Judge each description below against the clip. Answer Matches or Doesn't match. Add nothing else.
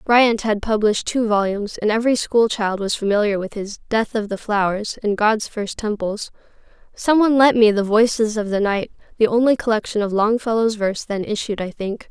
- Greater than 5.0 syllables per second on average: Matches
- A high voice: Matches